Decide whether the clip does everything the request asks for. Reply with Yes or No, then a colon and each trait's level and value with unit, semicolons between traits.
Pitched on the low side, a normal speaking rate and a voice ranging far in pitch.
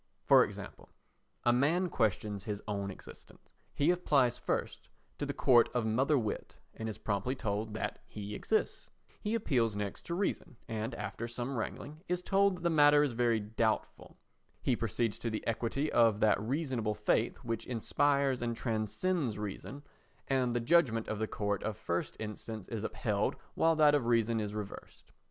No: low, 115 Hz; average, 170 wpm; average, 4.6 semitones